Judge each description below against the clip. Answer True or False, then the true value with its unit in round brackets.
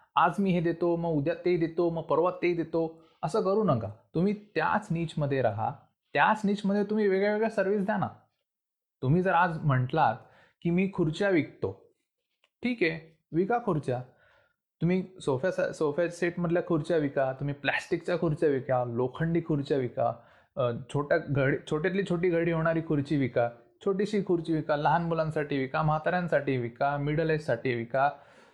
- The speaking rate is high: True (155 wpm)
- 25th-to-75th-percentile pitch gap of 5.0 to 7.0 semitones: False (4.5 semitones)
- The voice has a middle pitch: True (165 Hz)